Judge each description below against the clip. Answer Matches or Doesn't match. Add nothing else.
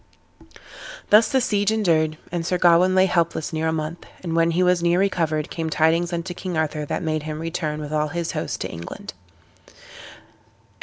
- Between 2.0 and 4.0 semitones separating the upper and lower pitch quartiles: Matches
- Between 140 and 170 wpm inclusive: Doesn't match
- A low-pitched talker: Doesn't match